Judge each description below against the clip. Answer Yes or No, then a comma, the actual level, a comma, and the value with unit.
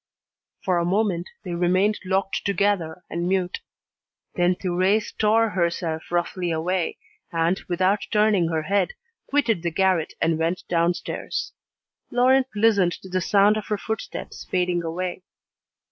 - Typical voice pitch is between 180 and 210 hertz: Yes, medium, 185 Hz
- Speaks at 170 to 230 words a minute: No, slow, 135 wpm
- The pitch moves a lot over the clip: No, average, 2.9 semitones